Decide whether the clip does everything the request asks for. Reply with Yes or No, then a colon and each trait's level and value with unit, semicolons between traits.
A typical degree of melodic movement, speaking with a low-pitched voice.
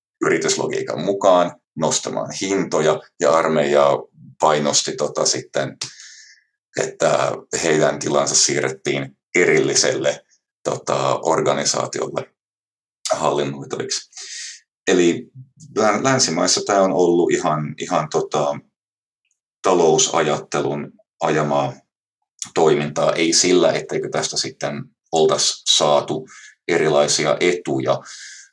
Yes: average, 3.3 semitones; very low, 75 Hz